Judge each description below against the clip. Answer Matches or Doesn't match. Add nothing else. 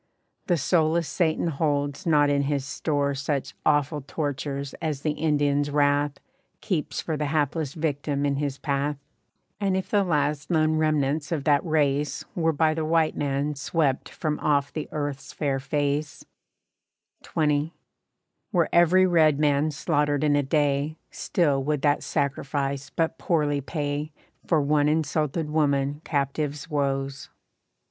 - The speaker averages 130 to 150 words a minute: Matches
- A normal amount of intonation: Doesn't match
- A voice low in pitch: Doesn't match